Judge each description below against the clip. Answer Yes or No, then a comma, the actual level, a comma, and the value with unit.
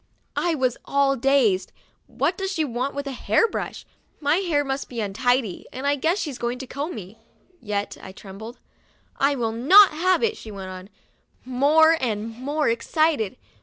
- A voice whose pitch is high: Yes, very high, 265 Hz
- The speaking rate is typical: Yes, average, 175 wpm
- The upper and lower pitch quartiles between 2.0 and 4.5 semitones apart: No, average, 5.2 semitones